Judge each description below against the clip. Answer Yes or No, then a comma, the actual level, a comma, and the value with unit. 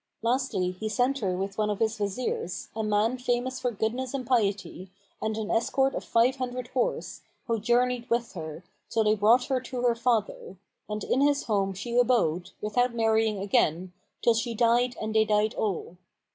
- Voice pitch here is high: Yes, high, 225 Hz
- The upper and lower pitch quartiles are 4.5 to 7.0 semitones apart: No, average, 3.1 semitones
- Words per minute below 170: No, average, 185 wpm